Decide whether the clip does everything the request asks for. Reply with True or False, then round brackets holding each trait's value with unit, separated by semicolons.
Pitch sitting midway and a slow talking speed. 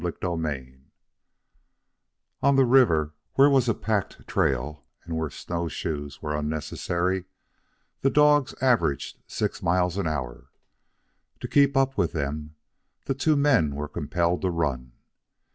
False (85 Hz; 130 wpm)